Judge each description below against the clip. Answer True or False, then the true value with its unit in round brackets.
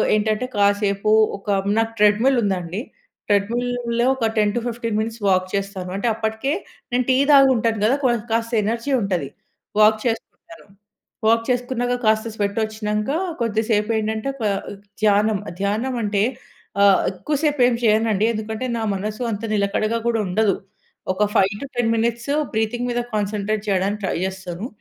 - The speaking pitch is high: True (220 Hz)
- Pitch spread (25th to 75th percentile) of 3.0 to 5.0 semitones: False (2.4 semitones)